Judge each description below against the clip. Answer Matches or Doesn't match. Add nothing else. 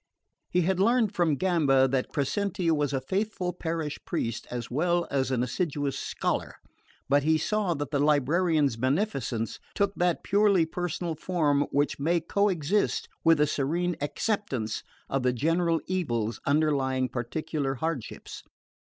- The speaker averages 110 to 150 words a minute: Matches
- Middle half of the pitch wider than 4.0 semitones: Matches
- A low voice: Doesn't match